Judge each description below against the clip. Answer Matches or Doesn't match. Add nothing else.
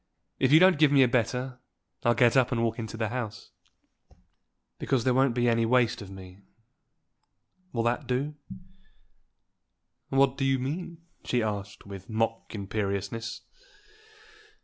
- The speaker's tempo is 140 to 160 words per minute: Matches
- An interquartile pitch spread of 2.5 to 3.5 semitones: Matches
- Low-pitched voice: Matches